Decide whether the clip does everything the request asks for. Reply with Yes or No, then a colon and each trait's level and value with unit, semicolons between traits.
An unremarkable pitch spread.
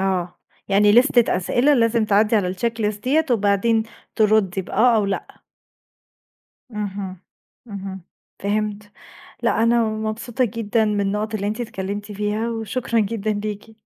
No: narrow, 2.2 semitones